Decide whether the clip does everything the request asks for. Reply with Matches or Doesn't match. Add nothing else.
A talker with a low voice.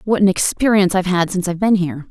Doesn't match